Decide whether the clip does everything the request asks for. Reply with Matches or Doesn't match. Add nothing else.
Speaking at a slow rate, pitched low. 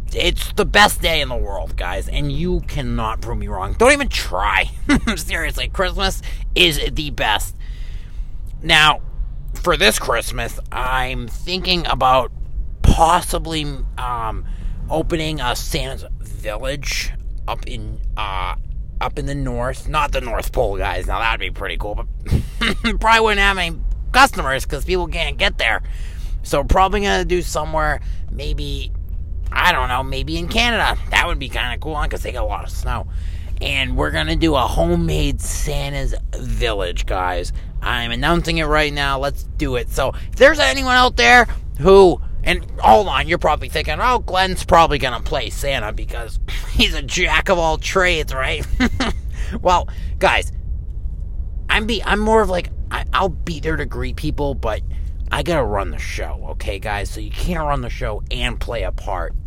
Doesn't match